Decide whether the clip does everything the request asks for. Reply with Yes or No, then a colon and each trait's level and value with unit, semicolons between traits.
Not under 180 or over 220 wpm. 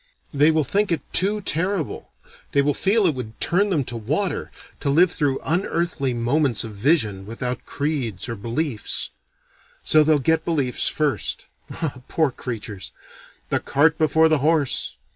No: average, 155 wpm